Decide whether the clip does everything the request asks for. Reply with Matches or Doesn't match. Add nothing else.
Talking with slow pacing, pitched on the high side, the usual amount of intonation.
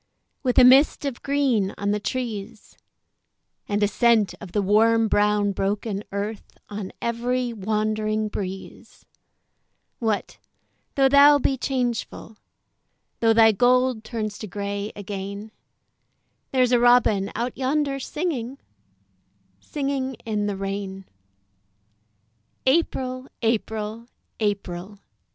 Matches